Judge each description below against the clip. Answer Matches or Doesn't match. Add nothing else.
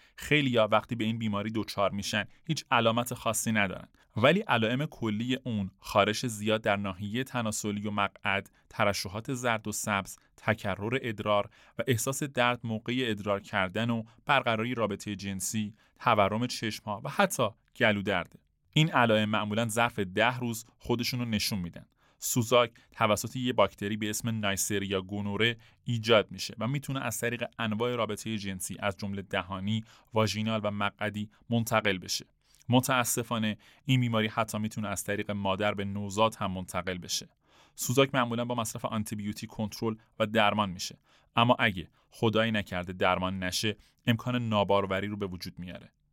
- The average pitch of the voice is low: Matches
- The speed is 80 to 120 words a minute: Doesn't match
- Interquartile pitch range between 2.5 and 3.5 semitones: Matches